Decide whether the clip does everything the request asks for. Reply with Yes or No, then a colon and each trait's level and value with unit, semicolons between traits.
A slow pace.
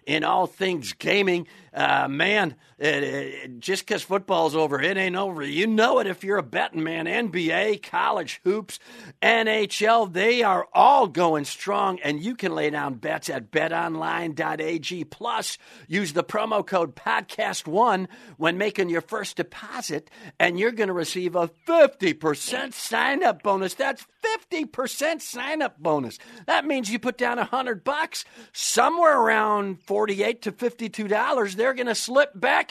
No: average, 150 wpm